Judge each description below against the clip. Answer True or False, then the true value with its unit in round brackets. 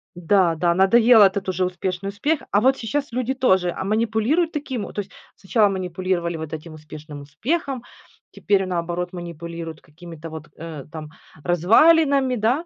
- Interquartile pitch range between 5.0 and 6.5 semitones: True (5.6 semitones)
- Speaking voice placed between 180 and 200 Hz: True (190 Hz)